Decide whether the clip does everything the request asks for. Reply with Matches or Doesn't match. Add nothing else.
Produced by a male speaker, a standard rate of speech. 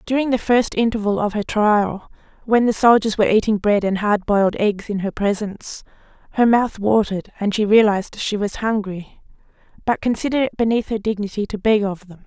Doesn't match